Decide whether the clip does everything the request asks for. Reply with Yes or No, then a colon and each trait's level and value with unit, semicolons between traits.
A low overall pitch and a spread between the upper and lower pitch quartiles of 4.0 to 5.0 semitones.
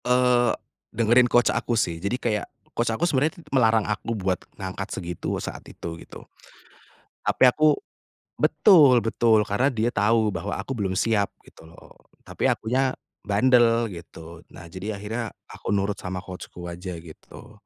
Yes: low, 110 Hz; average, 4.5 semitones